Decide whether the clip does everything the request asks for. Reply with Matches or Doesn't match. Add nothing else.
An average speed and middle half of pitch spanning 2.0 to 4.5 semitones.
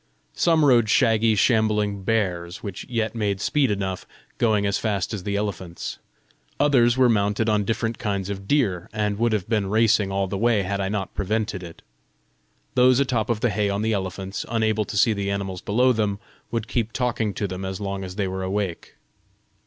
Matches